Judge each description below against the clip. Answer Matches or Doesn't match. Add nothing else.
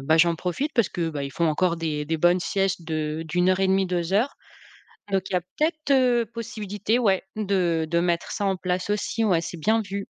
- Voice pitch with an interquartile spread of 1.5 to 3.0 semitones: Doesn't match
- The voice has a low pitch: Doesn't match